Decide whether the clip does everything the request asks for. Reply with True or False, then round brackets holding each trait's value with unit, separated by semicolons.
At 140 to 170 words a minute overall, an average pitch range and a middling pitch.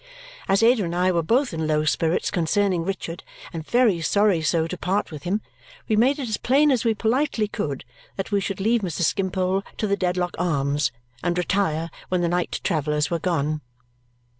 False (190 wpm; 4.1 semitones; 180 Hz)